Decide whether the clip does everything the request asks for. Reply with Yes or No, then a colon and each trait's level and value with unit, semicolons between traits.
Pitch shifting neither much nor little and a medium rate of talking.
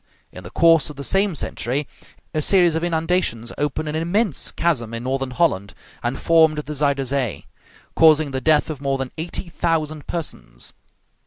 Yes: average, 3.7 semitones; average, 170 wpm